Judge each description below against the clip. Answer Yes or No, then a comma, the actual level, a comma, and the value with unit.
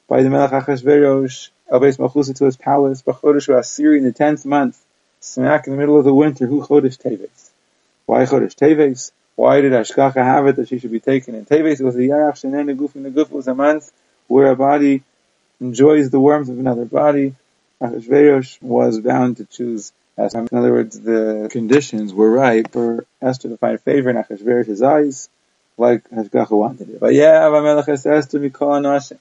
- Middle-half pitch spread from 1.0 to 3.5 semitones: Yes, average, 2.9 semitones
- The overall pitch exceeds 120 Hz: Yes, low, 135 Hz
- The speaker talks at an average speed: Yes, average, 195 wpm